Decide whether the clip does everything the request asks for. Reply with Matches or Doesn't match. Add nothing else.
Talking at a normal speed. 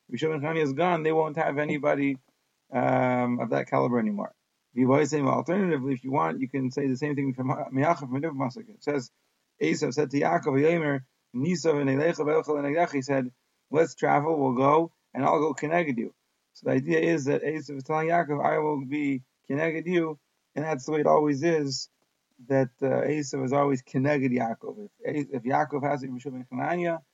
Matches